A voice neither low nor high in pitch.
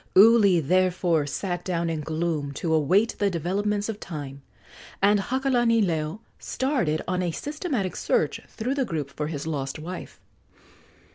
Yes: medium, 180 Hz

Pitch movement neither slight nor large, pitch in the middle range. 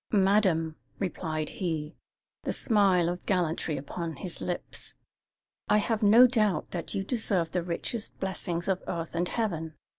Yes: average, 3.8 semitones; medium, 180 Hz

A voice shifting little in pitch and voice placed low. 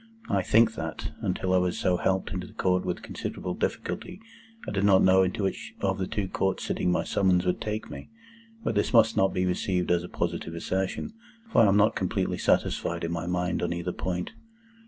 Yes: narrow, 2.0 semitones; very low, 95 Hz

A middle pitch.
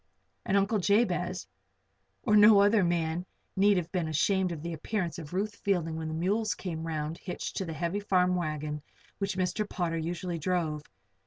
Yes: medium, 180 Hz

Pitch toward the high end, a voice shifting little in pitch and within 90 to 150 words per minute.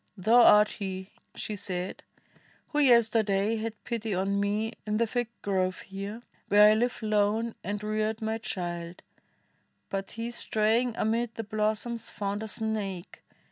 Yes: high, 215 Hz; narrow, 2.1 semitones; average, 145 wpm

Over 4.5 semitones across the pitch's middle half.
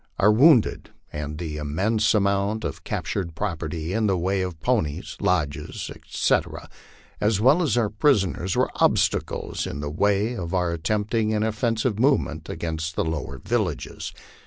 Yes: average, 5.1 semitones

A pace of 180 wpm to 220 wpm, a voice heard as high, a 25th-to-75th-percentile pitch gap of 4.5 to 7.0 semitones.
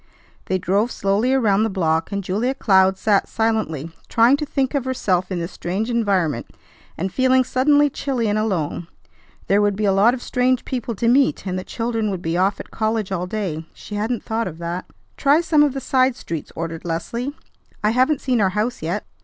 Yes: fast, 205 wpm; high, 215 Hz; average, 5.1 semitones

